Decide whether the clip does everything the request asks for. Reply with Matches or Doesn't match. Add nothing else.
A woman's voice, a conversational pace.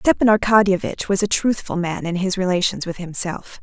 Matches